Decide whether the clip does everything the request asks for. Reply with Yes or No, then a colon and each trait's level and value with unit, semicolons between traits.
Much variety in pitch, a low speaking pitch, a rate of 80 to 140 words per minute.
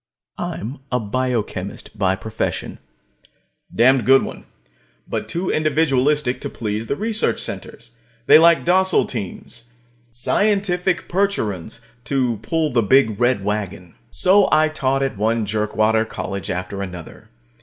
Yes: wide, 6.5 semitones; low, 125 Hz; slow, 135 wpm